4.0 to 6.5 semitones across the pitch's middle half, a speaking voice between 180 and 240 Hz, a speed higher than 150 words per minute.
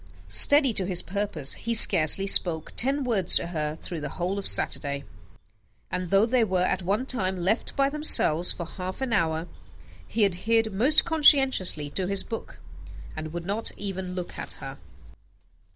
Yes: average, 4.8 semitones; high, 190 Hz; average, 170 wpm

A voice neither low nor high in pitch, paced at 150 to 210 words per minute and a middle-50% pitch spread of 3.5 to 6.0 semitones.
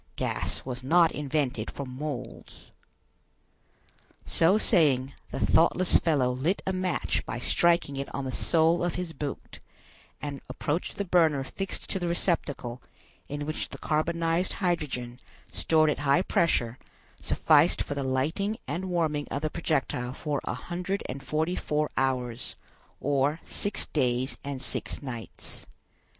No: medium, 150 Hz; average, 140 wpm; average, 4.2 semitones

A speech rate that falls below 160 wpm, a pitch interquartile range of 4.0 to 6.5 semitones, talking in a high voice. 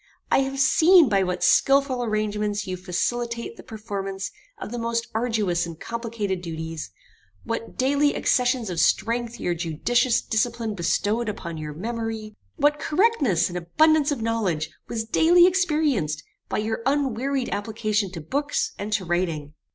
Yes: average, 145 wpm; wide, 5.5 semitones; high, 225 Hz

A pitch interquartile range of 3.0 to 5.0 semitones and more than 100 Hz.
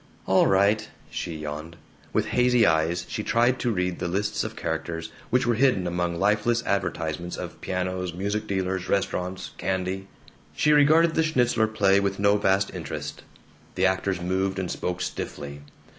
No: average, 3.5 semitones; very low, 95 Hz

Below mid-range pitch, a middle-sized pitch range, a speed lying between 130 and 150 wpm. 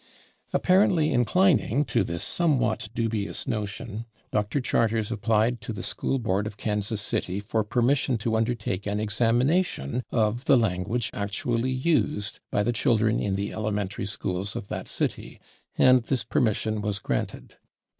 Yes: low, 110 Hz; average, 3.1 semitones; average, 145 wpm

